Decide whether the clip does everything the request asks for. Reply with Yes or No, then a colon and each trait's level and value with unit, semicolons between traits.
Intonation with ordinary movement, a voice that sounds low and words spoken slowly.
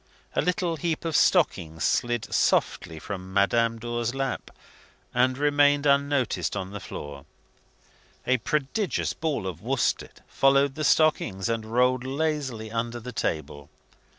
Yes: average, 5.0 semitones; low, 125 Hz; slow, 130 wpm